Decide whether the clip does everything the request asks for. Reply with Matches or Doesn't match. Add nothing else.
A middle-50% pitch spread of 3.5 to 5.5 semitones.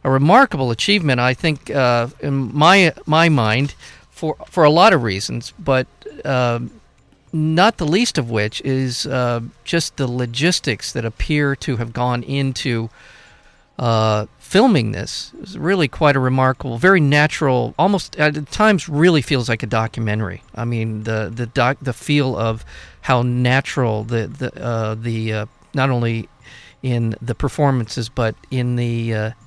Matches